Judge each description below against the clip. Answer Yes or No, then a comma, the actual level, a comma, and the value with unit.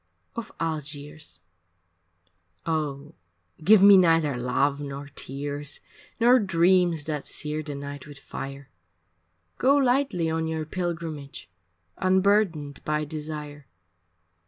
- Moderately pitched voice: Yes, medium, 155 Hz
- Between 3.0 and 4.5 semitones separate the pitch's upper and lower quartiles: Yes, average, 3.6 semitones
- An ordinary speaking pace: No, slow, 110 wpm